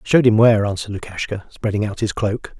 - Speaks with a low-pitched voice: Yes, low, 105 Hz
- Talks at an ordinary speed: No, fast, 210 wpm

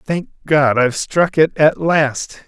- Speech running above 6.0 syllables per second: No, 3.7 syllables/s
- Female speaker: No, male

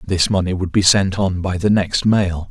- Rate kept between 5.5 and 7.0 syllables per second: No, 4.6 syllables/s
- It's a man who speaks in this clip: Yes, male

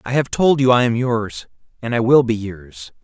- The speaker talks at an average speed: No, fast, 235 wpm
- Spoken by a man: Yes, male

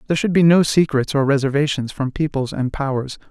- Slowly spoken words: No, average, 200 wpm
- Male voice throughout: Yes, male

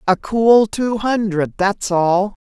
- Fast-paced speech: No, average, 145 wpm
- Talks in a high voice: Yes, high, 205 Hz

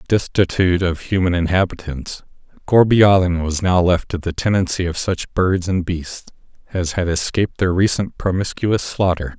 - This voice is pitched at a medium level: No, very low, 90 Hz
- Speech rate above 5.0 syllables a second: No, 4.9 syllables/s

